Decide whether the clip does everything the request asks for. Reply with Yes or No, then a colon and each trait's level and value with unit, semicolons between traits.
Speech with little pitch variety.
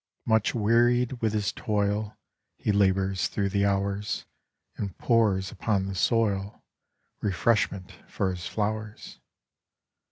Yes: narrow, 2.1 semitones